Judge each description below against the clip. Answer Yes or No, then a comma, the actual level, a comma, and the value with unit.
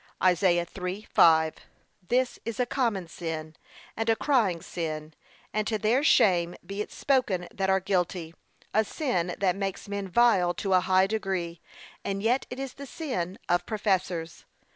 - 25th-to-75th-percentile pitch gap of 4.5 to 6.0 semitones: No, average, 4.0 semitones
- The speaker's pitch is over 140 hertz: Yes, high, 190 Hz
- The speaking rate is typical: Yes, average, 160 wpm